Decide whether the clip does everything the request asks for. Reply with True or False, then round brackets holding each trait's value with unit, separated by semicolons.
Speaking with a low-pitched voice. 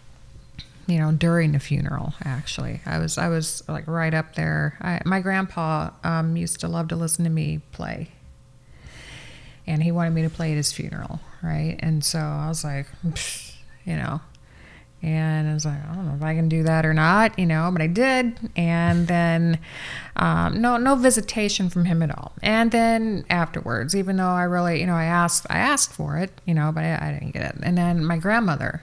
False (165 Hz)